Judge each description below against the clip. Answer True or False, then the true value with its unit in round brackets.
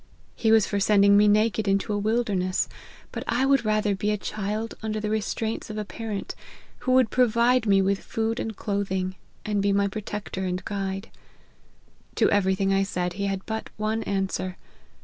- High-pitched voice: True (205 Hz)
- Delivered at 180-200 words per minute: True (185 wpm)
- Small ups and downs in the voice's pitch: True (2.1 semitones)